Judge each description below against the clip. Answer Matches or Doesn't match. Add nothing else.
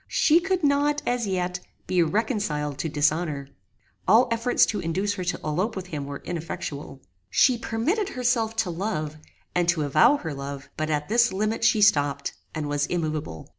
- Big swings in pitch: Matches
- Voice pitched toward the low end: Doesn't match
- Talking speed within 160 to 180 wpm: Matches